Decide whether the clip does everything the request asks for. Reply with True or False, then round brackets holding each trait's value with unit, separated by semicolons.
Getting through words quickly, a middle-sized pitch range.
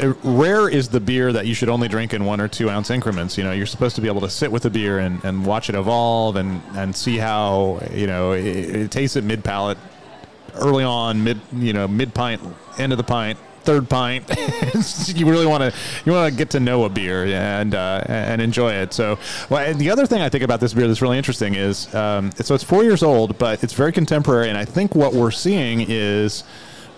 True (235 wpm; 4.5 semitones)